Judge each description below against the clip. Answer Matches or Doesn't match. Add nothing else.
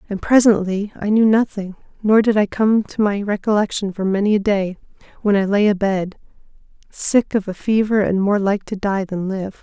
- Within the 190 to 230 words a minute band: Matches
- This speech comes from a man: Doesn't match